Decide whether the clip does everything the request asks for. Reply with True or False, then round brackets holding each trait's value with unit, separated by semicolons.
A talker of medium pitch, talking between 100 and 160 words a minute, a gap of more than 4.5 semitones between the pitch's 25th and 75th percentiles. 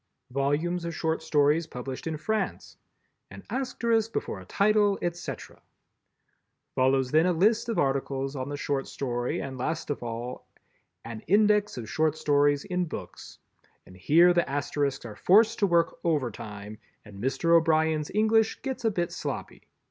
True (155 Hz; 155 wpm; 5.1 semitones)